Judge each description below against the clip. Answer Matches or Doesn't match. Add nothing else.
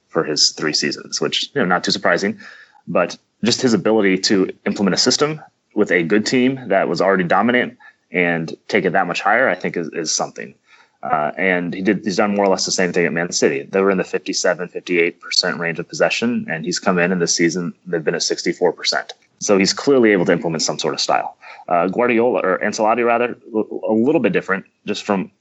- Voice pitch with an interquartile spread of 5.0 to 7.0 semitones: Doesn't match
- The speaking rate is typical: Doesn't match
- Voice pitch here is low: Matches